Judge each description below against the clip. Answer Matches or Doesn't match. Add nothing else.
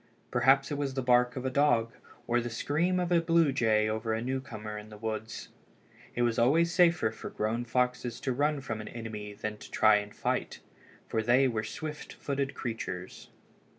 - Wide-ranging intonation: Doesn't match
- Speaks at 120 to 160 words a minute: Doesn't match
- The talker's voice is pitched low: Matches